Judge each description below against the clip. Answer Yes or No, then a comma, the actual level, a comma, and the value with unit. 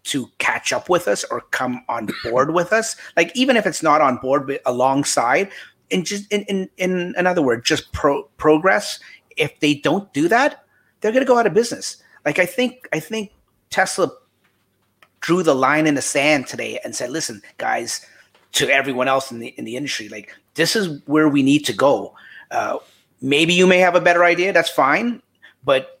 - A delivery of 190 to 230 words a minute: Yes, average, 195 wpm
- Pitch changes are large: Yes, wide, 6.2 semitones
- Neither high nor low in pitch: Yes, medium, 170 Hz